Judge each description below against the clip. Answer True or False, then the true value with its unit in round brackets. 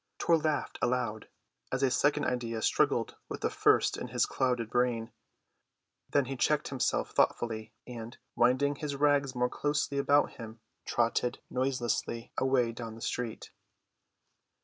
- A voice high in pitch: False (125 Hz)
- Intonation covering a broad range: False (3.1 semitones)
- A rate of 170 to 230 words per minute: False (140 wpm)